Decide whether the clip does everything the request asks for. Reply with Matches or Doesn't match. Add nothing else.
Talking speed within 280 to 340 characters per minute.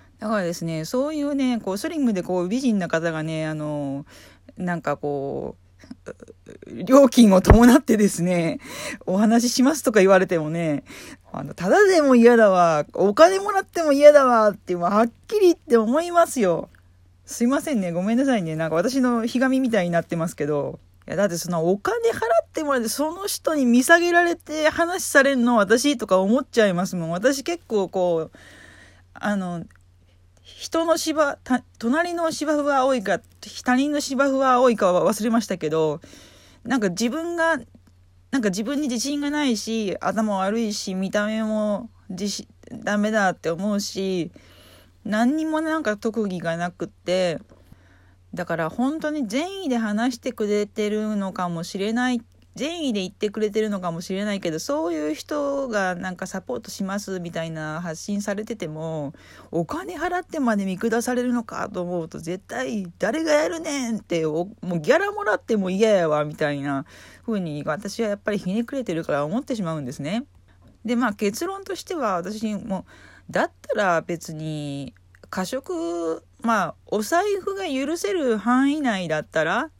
Matches